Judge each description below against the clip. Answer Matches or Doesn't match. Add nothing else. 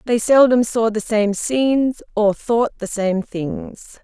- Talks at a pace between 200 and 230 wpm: Doesn't match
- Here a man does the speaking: Doesn't match